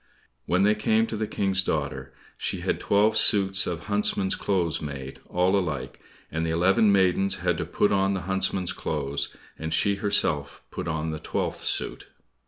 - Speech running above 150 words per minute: Yes, average, 175 wpm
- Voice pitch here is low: Yes, very low, 95 Hz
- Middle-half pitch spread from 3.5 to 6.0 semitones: Yes, average, 4.0 semitones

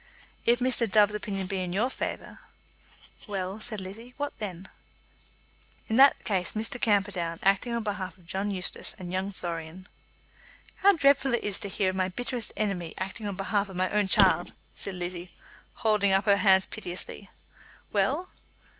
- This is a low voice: No, high, 200 Hz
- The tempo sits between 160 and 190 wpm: Yes, average, 170 wpm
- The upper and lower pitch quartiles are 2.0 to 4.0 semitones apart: Yes, average, 2.8 semitones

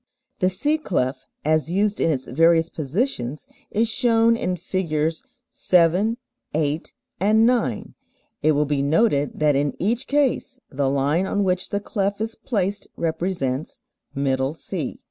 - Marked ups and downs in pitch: Yes, wide, 6.2 semitones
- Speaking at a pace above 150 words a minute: No, average, 145 wpm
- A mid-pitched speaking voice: Yes, medium, 170 Hz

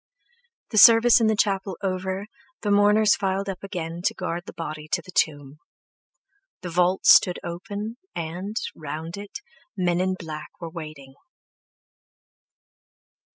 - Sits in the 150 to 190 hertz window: Yes, medium, 185 Hz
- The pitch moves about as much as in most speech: Yes, average, 3.5 semitones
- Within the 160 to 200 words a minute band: No, slow, 135 wpm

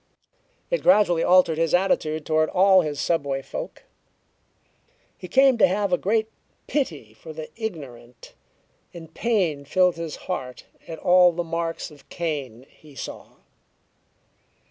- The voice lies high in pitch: No, medium, 165 Hz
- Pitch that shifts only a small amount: No, average, 3.7 semitones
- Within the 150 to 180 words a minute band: No, slow, 135 wpm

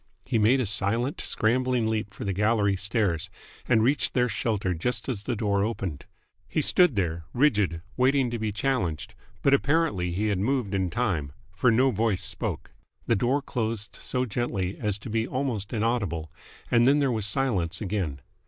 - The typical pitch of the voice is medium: No, low, 110 Hz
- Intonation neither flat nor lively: Yes, average, 4.2 semitones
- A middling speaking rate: Yes, average, 175 wpm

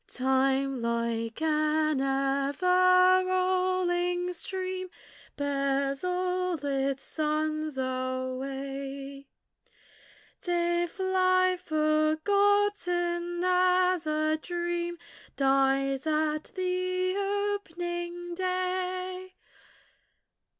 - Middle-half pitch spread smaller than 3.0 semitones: No, average, 4.9 semitones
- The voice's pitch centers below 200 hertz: No, very high, 345 Hz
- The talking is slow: Yes, slow, 65 wpm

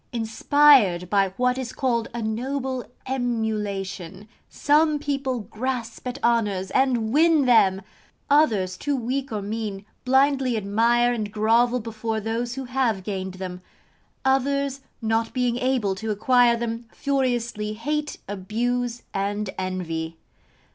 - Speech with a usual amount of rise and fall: Yes, average, 3.9 semitones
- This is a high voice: Yes, high, 235 Hz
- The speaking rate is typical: No, slow, 125 wpm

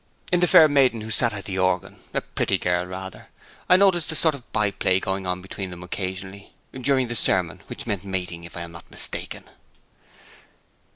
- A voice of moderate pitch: No, very low, 95 Hz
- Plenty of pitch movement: Yes, wide, 5.7 semitones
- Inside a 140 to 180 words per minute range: No, average, 195 wpm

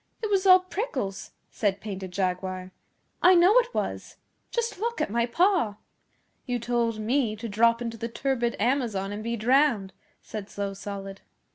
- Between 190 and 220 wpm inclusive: No, average, 160 wpm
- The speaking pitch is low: No, high, 230 Hz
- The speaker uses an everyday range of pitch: No, wide, 6.1 semitones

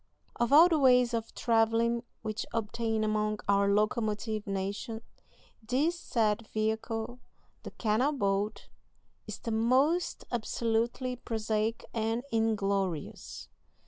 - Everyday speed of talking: No, slow, 110 wpm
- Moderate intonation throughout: No, narrow, 2.0 semitones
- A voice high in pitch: Yes, high, 225 Hz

